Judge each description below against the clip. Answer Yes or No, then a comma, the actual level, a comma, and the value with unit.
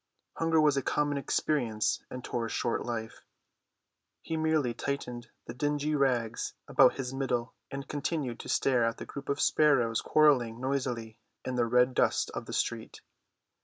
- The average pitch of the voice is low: Yes, low, 130 Hz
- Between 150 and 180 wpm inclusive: Yes, average, 160 wpm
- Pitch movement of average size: Yes, average, 3.5 semitones